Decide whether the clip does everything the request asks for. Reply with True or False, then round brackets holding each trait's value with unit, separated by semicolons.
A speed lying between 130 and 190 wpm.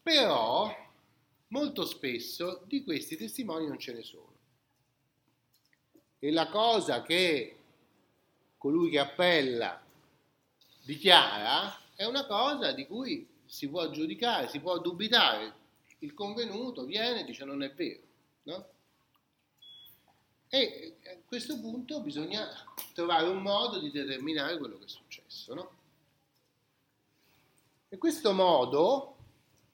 False (115 wpm)